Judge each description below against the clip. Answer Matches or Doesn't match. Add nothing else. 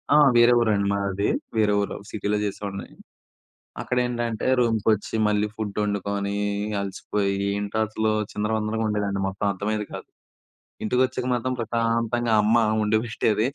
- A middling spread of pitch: Doesn't match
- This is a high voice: Doesn't match